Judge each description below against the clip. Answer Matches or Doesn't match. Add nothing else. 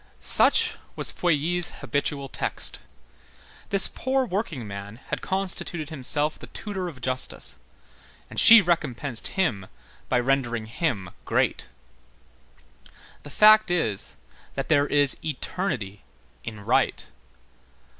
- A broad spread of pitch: Matches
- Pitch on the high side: Doesn't match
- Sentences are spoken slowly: Matches